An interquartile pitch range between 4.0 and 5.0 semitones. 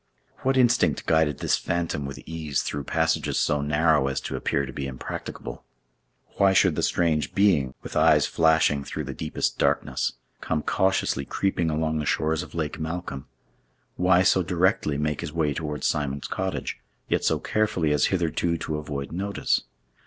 No: average, 3.4 semitones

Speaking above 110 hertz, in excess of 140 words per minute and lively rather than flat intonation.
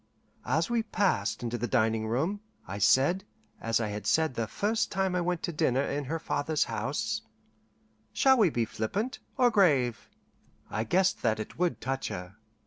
Yes: medium, 140 Hz; average, 175 wpm; wide, 9.0 semitones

